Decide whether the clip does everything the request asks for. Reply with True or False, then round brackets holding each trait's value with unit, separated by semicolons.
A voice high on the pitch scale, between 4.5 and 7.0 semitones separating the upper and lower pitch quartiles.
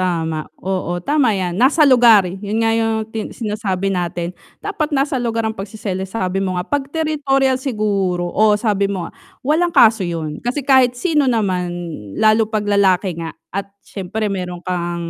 True (210 Hz; 4.9 semitones)